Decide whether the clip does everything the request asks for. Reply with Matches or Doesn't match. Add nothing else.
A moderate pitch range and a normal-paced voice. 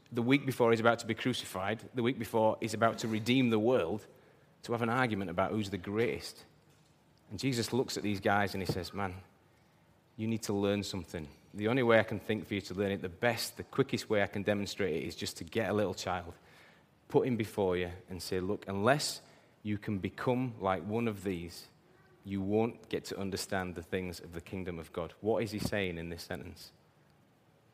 Doesn't match